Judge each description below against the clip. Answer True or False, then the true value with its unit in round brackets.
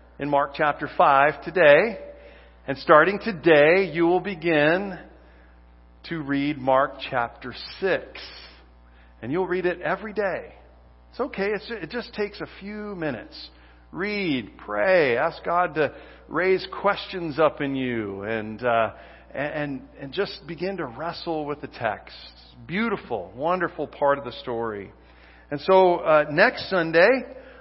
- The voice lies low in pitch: False (145 Hz)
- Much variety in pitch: True (8.8 semitones)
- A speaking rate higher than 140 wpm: False (135 wpm)